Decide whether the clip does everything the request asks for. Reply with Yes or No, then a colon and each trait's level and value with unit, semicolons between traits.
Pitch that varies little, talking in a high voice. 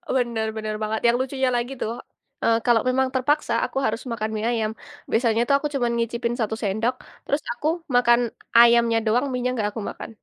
Yes: narrow, 2.2 semitones; high, 235 Hz